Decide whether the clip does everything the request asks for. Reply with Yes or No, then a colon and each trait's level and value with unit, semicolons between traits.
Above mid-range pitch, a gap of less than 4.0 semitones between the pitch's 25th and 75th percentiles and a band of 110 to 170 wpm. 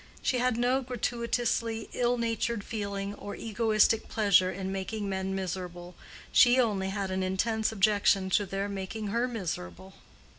Yes: high, 205 Hz; average, 3.3 semitones; average, 145 wpm